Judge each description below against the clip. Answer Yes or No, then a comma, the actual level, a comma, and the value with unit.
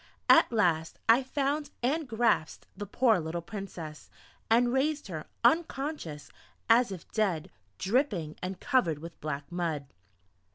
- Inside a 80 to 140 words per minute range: Yes, slow, 135 wpm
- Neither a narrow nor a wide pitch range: No, wide, 7.8 semitones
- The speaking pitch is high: Yes, high, 205 Hz